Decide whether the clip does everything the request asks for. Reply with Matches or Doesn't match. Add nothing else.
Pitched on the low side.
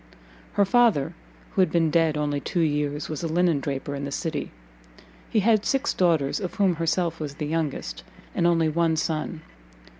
Doesn't match